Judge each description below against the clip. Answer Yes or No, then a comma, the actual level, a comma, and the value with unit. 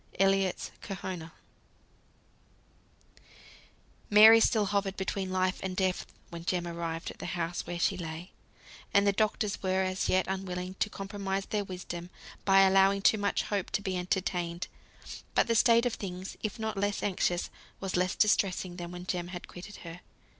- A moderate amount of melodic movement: No, narrow, 2.0 semitones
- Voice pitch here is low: No, high, 190 Hz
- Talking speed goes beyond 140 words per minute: Yes, average, 160 wpm